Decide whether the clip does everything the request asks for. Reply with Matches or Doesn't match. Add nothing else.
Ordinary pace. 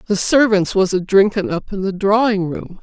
Matches